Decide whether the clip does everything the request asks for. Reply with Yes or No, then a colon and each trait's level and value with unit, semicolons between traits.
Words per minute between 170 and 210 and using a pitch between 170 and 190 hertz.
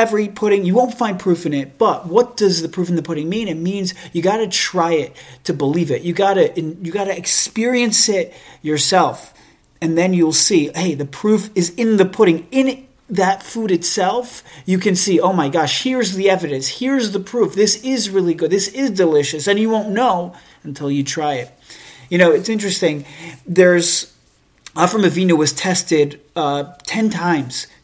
Yes: average, 185 wpm; medium, 185 Hz